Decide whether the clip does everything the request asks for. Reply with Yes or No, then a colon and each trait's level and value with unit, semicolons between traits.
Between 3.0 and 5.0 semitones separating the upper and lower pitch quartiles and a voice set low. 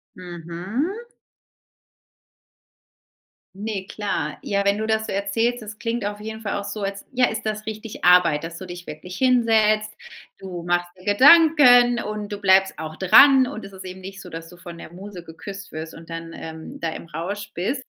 No: average, 3.8 semitones; high, 200 Hz